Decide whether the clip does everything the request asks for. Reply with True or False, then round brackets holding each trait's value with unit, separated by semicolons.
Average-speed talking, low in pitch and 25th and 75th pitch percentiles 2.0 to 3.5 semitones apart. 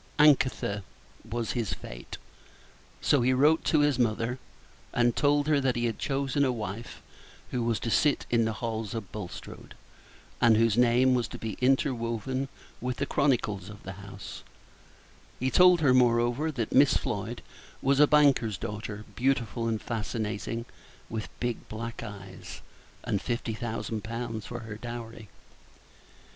True (150 wpm; 120 Hz; 3.0 semitones)